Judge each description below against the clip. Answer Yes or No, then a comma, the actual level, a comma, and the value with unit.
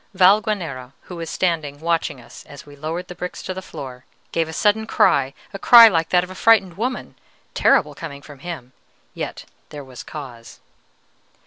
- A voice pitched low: No, medium, 165 Hz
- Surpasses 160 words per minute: Yes, average, 180 wpm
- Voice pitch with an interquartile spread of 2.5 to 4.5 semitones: No, average, 4.9 semitones